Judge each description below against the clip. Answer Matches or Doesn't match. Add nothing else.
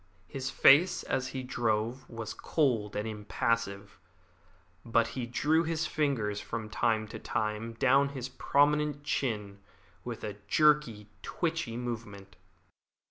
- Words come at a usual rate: Doesn't match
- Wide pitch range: Doesn't match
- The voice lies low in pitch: Matches